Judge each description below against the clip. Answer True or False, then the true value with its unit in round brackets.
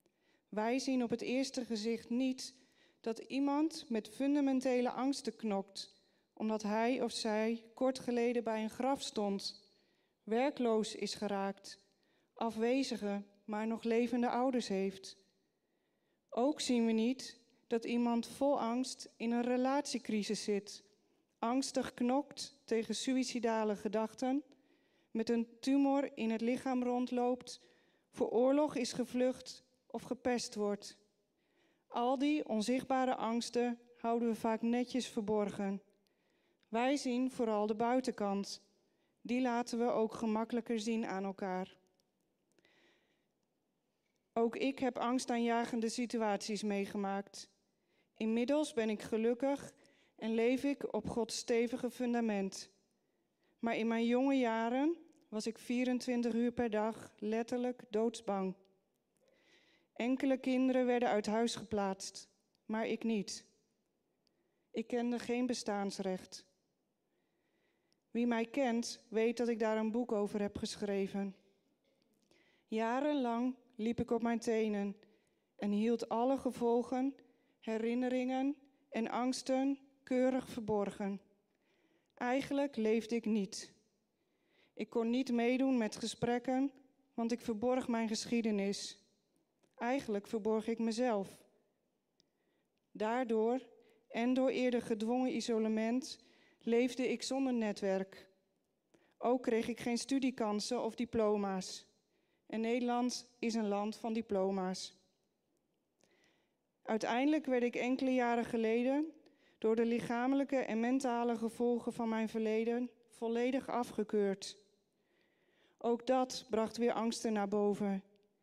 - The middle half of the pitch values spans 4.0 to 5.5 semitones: False (2.6 semitones)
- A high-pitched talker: True (235 Hz)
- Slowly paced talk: True (110 wpm)